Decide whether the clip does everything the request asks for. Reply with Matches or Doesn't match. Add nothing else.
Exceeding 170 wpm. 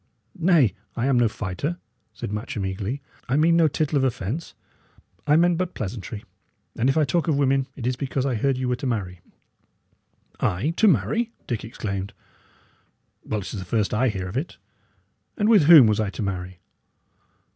Matches